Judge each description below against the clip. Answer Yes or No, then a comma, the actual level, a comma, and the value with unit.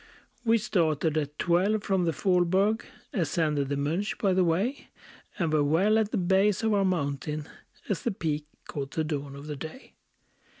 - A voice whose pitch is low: No, medium, 170 Hz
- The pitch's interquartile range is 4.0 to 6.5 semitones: Yes, average, 4.8 semitones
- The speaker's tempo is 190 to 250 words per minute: No, average, 175 wpm